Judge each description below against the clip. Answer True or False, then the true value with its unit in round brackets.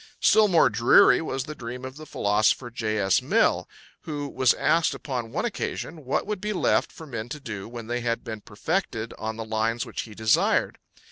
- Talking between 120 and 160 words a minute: False (200 wpm)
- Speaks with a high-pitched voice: False (120 Hz)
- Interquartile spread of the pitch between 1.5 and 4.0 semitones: False (5.4 semitones)